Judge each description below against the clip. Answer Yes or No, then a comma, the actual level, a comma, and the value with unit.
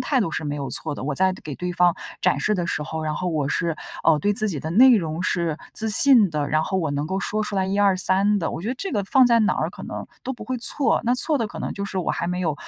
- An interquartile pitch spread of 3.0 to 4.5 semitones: No, average, 5.2 semitones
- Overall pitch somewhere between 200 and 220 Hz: No, high, 190 Hz